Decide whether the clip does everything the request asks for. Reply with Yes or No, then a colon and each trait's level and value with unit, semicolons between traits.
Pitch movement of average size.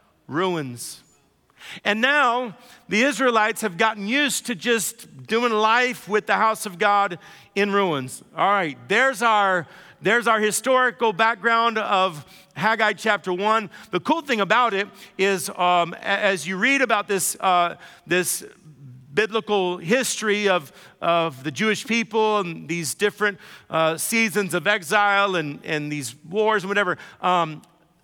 Yes: average, 3.8 semitones